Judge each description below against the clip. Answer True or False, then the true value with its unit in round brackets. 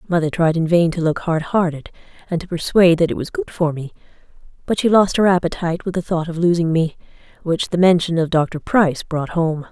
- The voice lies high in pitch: False (165 Hz)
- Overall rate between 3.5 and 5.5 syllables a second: False (5.8 syllables/s)